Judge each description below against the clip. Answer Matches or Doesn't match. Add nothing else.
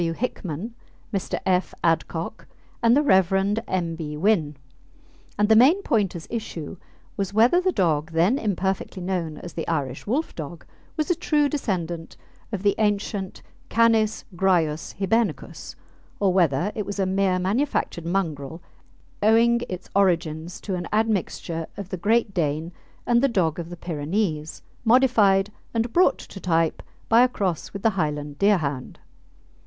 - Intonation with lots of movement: Doesn't match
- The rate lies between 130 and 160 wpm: Matches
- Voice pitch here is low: Doesn't match